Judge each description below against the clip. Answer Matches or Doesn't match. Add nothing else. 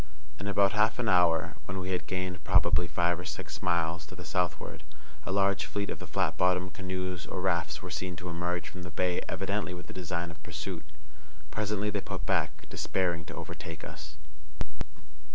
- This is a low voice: Matches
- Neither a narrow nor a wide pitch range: Doesn't match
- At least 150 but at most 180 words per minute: Doesn't match